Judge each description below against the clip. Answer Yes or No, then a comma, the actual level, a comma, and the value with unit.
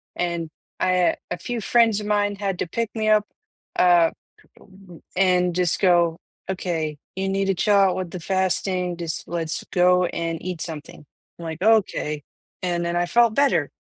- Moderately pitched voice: Yes, medium, 180 Hz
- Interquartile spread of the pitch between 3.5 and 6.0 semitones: No, narrow, 2.6 semitones